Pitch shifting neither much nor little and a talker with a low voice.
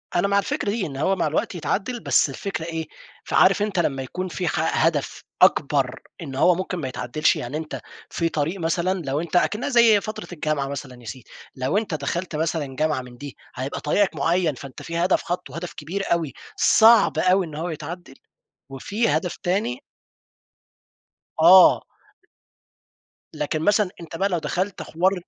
No: average, 4.3 semitones; medium, 165 Hz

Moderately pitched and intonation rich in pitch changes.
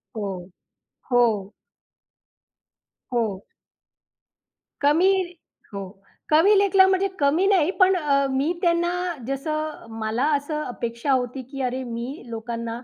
No: very high, 275 Hz; wide, 6.4 semitones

